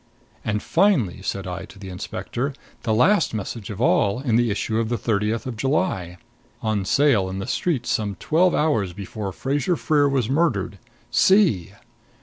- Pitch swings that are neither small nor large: No, wide, 6.2 semitones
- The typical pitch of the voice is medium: No, low, 115 Hz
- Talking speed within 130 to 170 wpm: Yes, average, 165 wpm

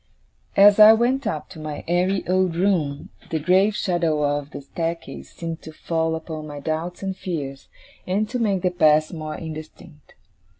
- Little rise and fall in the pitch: No, average, 3.4 semitones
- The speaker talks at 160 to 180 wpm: Yes, average, 170 wpm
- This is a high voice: No, medium, 165 Hz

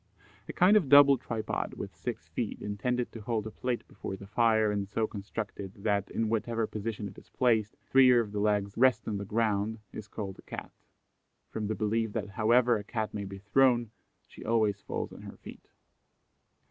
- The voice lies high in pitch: No, low, 110 Hz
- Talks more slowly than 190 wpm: No, average, 195 wpm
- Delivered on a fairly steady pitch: Yes, narrow, 2.3 semitones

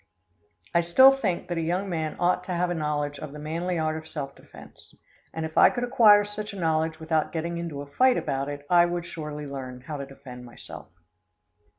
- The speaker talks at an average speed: No, fast, 215 wpm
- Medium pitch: Yes, medium, 160 Hz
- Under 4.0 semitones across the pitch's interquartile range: Yes, average, 3.3 semitones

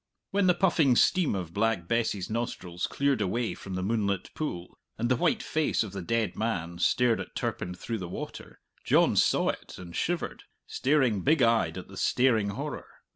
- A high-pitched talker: No, low, 115 Hz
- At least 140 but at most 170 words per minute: No, average, 180 wpm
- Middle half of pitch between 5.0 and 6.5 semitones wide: Yes, wide, 5.6 semitones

